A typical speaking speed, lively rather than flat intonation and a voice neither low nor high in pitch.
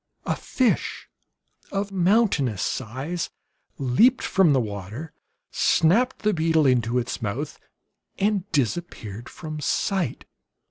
No: slow, 105 wpm; wide, 7.8 semitones; medium, 155 Hz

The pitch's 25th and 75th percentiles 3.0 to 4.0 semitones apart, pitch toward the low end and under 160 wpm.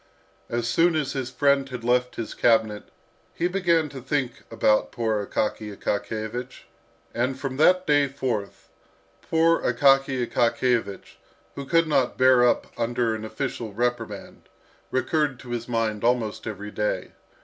Yes: average, 3.5 semitones; low, 125 Hz; average, 140 wpm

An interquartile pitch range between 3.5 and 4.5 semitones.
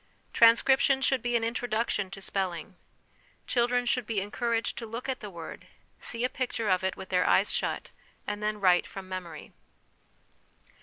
Yes: average, 4.1 semitones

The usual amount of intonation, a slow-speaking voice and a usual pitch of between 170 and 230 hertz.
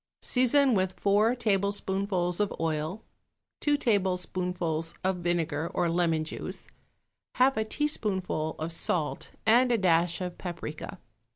Yes: average, 4.3 semitones; slow, 120 wpm; medium, 185 Hz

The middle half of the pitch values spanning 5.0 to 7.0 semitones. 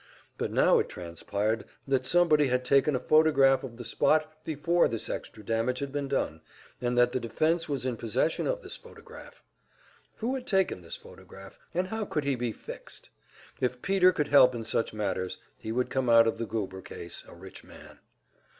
Yes: average, 5.3 semitones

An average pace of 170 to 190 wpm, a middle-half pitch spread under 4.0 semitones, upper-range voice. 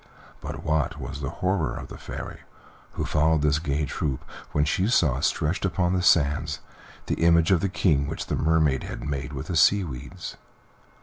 No: average, 185 wpm; average, 3.1 semitones; very low, 80 Hz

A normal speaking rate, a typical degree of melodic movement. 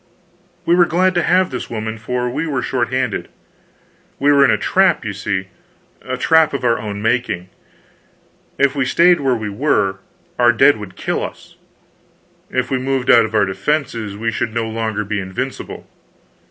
Yes: average, 180 wpm; average, 4.5 semitones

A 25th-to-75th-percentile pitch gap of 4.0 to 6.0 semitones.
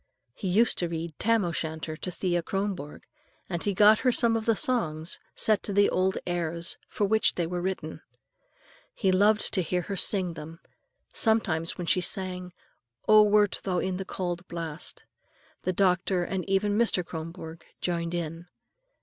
No: average, 3.2 semitones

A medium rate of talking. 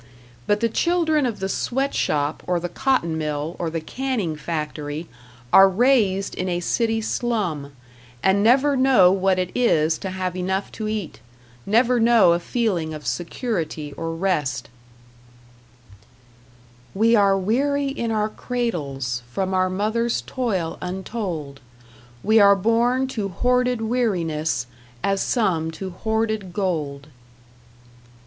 No: slow, 130 wpm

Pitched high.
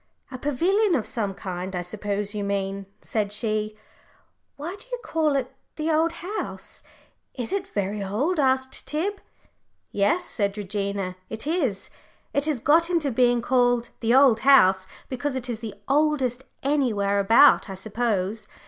Yes: high, 240 Hz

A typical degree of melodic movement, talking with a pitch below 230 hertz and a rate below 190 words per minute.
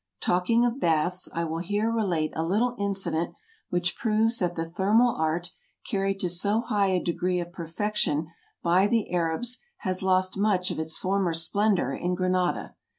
Yes: average, 3.3 semitones; medium, 185 Hz; average, 170 wpm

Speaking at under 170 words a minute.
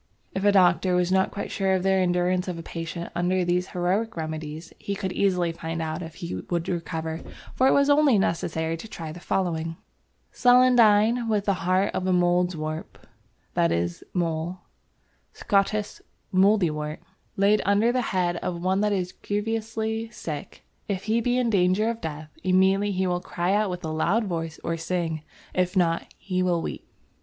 No: average, 175 wpm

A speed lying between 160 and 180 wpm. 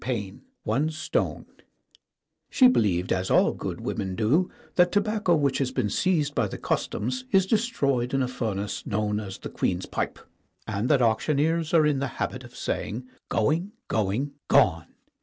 Yes: average, 165 wpm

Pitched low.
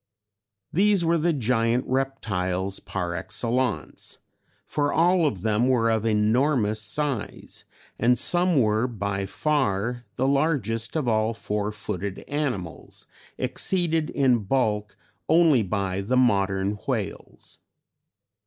Yes: low, 115 Hz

